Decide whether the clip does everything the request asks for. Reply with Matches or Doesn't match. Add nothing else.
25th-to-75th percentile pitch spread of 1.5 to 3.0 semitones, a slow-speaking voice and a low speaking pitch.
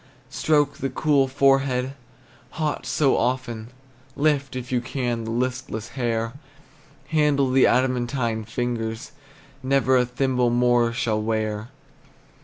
Matches